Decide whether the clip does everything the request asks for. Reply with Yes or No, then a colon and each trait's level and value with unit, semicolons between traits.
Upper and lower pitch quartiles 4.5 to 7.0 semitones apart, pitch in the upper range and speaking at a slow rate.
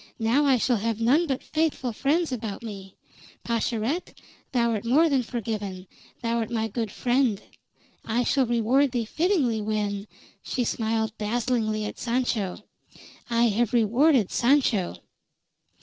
No: average, 3.0 semitones; high, 235 Hz; slow, 130 wpm